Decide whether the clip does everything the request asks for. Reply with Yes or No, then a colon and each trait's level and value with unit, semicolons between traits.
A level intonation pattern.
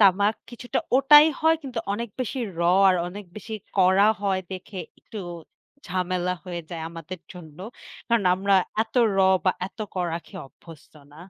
No: average, 3.6 semitones